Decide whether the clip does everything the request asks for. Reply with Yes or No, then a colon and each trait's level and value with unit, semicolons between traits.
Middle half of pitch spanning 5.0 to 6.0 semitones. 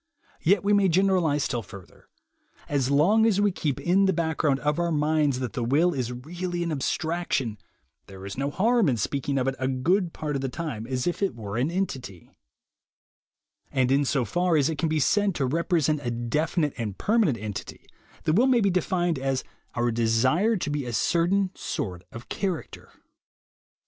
Yes: wide, 5.6 semitones